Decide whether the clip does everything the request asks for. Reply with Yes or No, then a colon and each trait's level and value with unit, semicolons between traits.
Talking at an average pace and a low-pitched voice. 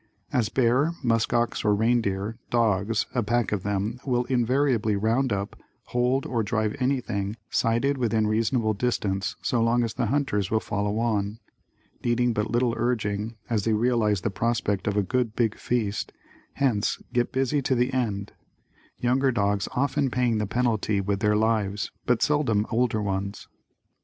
Yes: average, 155 wpm; low, 115 Hz